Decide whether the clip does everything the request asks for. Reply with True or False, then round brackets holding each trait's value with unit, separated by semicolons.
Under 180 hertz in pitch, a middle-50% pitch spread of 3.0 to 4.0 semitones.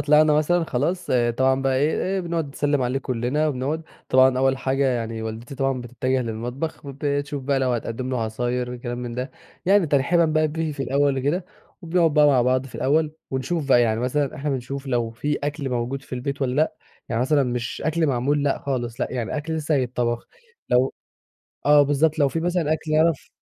True (135 Hz; 3.3 semitones)